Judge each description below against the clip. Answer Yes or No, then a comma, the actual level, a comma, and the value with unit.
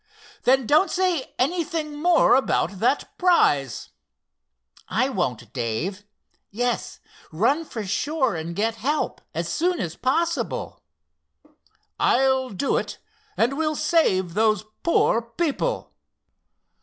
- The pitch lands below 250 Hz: No, very high, 255 Hz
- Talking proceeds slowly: Yes, slow, 105 wpm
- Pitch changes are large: Yes, wide, 8.2 semitones